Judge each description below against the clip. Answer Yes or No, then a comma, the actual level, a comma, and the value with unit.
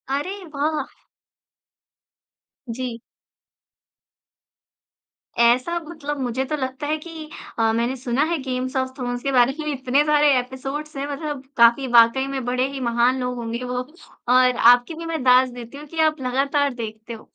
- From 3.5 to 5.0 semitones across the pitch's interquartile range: No, average, 2.9 semitones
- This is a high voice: Yes, very high, 260 Hz